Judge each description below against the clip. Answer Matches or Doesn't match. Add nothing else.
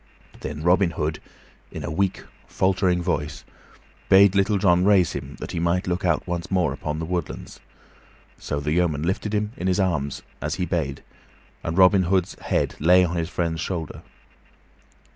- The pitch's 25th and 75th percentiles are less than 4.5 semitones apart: Matches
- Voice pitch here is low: Matches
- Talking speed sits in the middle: Matches